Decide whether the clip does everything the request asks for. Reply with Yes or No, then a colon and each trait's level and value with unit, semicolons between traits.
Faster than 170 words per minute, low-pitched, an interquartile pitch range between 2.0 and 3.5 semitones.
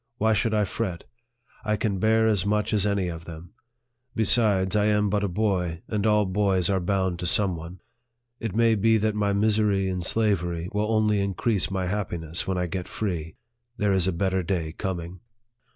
Yes: average, 190 wpm; low, 100 Hz; average, 2.9 semitones